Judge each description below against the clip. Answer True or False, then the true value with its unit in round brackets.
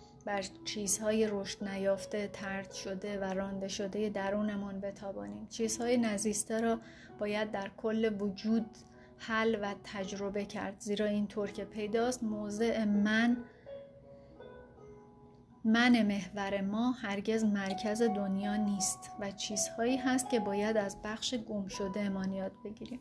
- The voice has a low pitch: False (205 Hz)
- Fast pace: False (125 wpm)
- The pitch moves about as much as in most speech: False (1.9 semitones)